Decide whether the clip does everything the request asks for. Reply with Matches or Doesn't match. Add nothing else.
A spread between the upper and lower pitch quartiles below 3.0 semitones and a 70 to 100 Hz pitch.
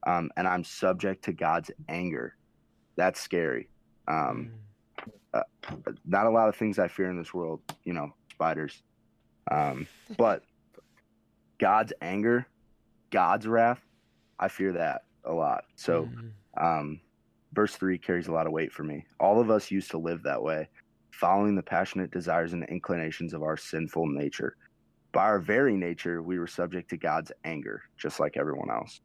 Doesn't match